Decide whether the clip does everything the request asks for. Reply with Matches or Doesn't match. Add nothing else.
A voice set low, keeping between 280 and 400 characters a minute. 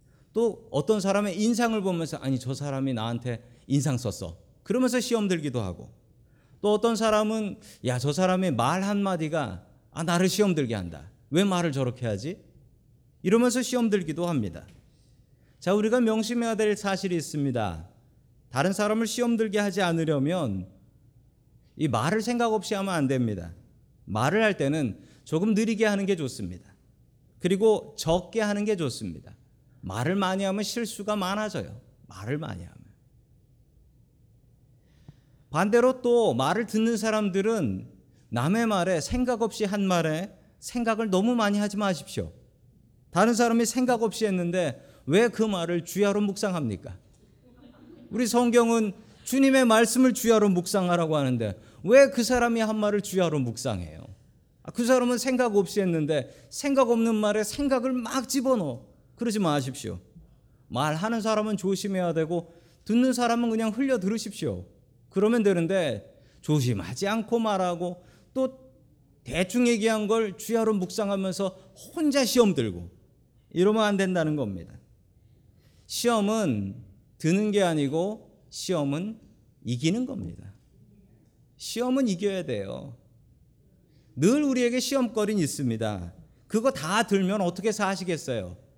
Doesn't match